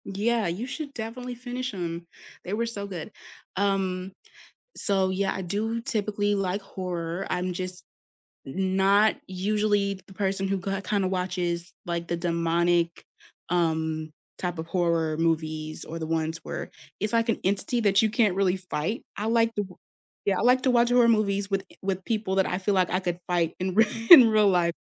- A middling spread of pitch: Yes, average, 3.4 semitones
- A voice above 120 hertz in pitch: Yes, high, 190 Hz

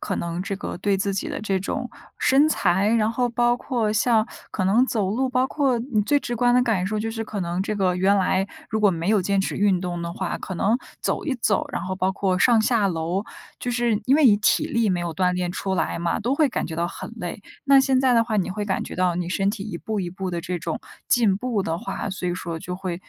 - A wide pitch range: No, average, 4.3 semitones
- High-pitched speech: Yes, high, 200 Hz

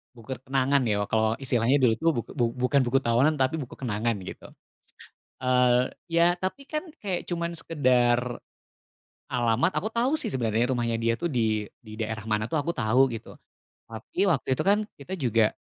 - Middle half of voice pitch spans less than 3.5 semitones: No, wide, 5.5 semitones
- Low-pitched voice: Yes, low, 125 Hz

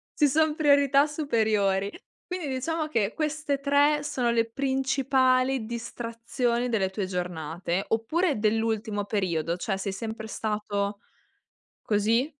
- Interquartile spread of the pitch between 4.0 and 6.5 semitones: Yes, wide, 5.4 semitones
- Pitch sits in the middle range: No, high, 230 Hz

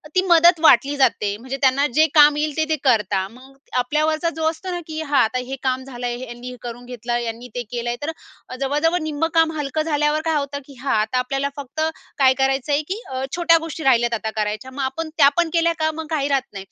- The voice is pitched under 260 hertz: No, very high, 280 Hz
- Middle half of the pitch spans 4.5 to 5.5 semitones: No, average, 4.0 semitones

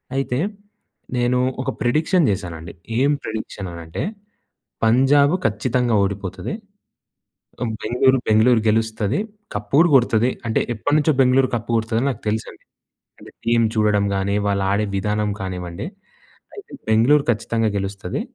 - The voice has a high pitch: No, low, 110 Hz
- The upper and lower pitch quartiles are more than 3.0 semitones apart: Yes, average, 4.0 semitones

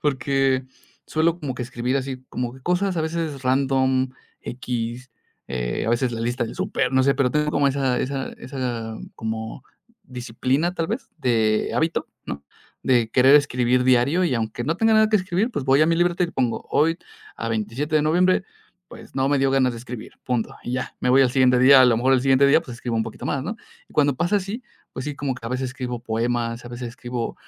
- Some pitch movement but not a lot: Yes, average, 3.3 semitones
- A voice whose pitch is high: No, low, 130 Hz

